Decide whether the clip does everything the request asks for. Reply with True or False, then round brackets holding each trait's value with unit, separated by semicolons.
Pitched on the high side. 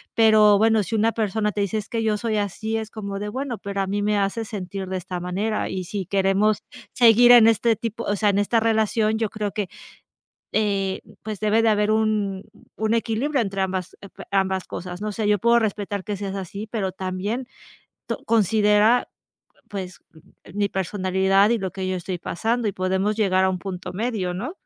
True (205 Hz)